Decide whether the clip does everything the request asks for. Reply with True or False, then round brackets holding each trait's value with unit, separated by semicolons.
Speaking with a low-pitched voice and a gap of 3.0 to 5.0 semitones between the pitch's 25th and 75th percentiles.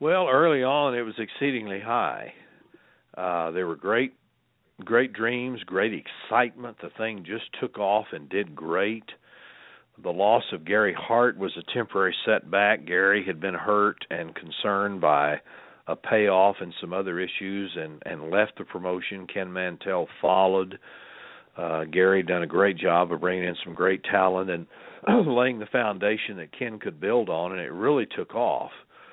True (95 Hz; 3.4 semitones)